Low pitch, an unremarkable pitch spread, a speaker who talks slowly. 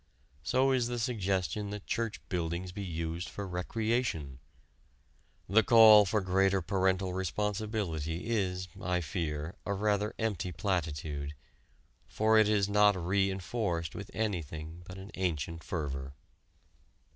Yes: very low, 95 Hz; average, 4.0 semitones; slow, 125 wpm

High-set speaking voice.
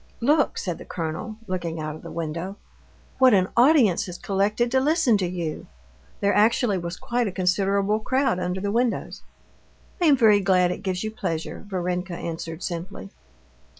Yes: high, 195 Hz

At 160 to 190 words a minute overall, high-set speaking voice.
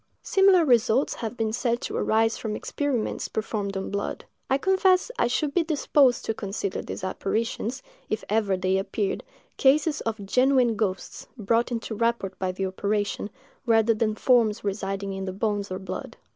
Yes: average, 165 wpm; high, 220 Hz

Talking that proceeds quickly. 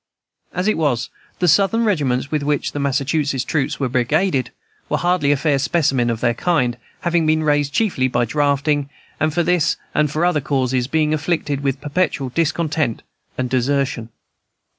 No: average, 160 wpm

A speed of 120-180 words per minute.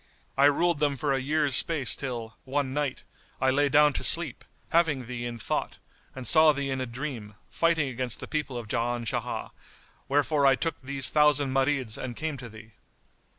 No: average, 190 wpm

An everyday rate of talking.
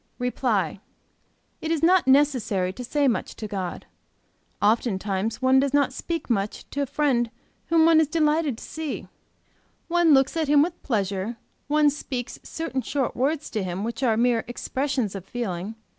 Yes: average, 165 wpm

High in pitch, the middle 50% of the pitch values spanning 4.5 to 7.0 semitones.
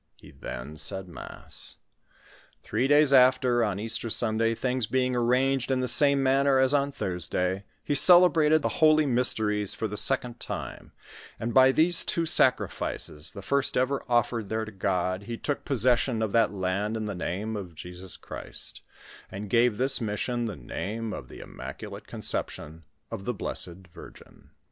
No: low, 115 Hz; average, 4.9 semitones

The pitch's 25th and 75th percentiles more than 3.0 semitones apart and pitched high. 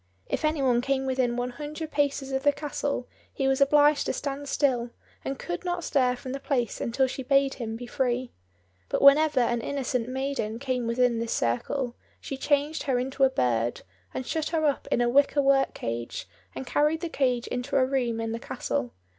No: average, 2.7 semitones; very high, 265 Hz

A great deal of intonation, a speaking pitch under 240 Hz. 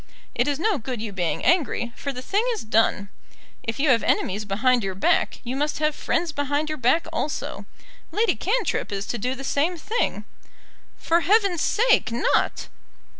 No: wide, 6.4 semitones; very high, 280 Hz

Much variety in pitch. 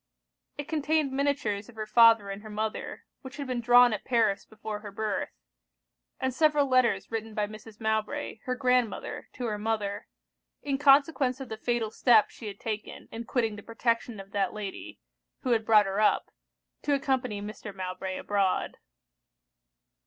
No: average, 3.4 semitones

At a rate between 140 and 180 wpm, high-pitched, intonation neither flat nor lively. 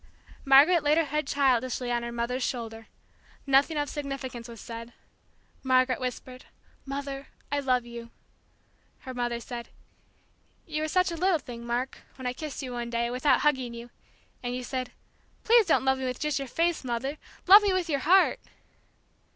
Yes: average, 175 wpm; very high, 260 Hz; average, 3.5 semitones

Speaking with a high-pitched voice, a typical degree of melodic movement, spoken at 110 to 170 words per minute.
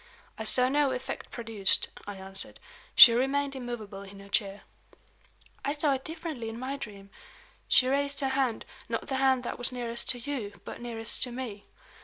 No: high, 245 Hz; average, 4.0 semitones; average, 180 wpm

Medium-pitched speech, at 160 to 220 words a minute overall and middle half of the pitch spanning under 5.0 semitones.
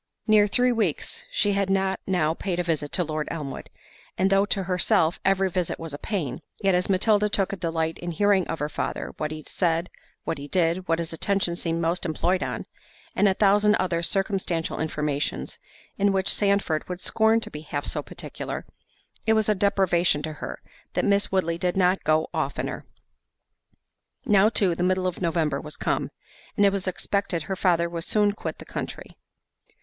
Yes: medium, 180 Hz; average, 190 wpm; average, 3.3 semitones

